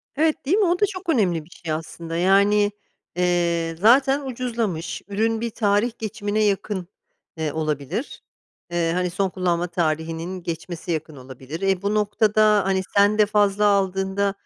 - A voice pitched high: Yes, high, 195 Hz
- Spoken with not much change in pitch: No, average, 4.0 semitones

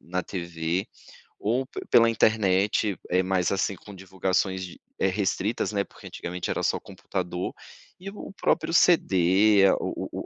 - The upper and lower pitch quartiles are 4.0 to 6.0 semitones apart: No, narrow, 2.5 semitones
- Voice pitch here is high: No, very low, 95 Hz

